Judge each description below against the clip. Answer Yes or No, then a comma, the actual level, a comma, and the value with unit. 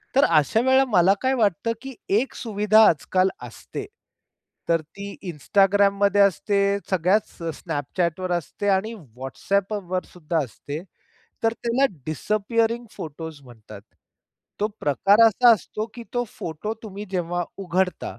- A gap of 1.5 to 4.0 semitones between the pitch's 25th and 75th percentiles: No, average, 4.5 semitones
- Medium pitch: No, high, 195 Hz